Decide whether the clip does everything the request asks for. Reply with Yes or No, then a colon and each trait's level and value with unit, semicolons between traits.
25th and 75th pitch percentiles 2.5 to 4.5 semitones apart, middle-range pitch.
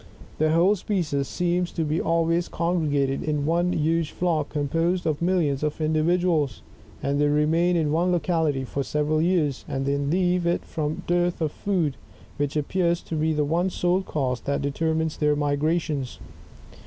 Yes: average, 2.9 semitones; medium, 160 Hz